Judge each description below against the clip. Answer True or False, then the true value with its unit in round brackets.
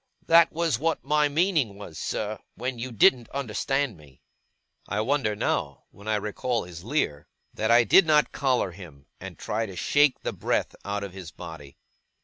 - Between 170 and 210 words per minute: True (175 wpm)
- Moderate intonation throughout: False (6.5 semitones)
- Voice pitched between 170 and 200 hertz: False (110 Hz)